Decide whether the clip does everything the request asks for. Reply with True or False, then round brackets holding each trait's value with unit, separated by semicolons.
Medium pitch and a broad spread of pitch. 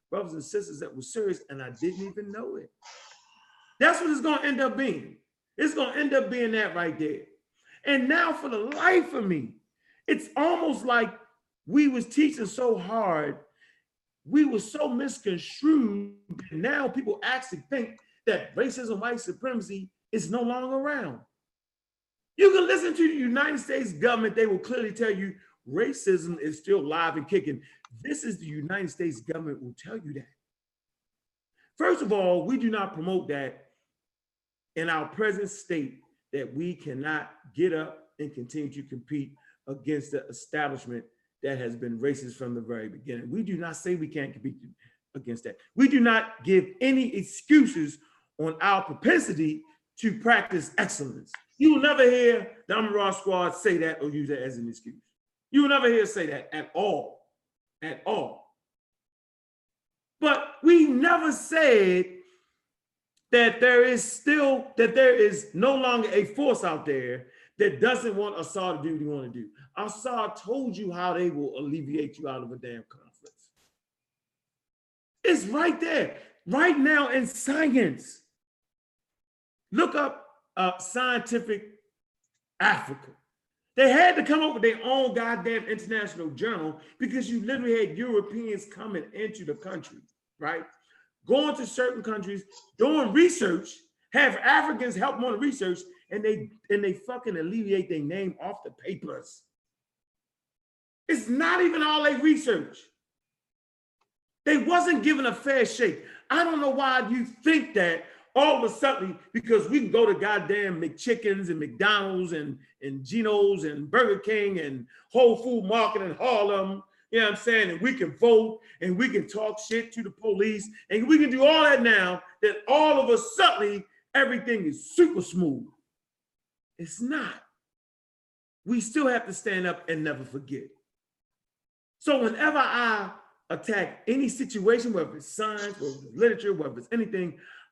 False (225 Hz; 7.4 semitones)